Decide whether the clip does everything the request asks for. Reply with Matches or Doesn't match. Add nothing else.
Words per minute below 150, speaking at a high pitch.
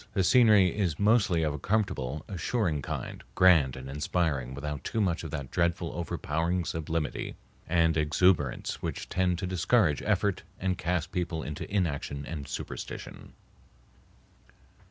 Doesn't match